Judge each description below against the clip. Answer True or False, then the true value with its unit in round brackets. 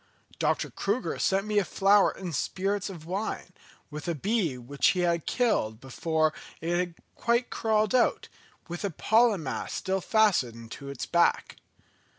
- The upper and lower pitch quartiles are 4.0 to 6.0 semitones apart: True (5.0 semitones)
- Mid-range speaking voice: True (180 Hz)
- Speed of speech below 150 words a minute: False (160 wpm)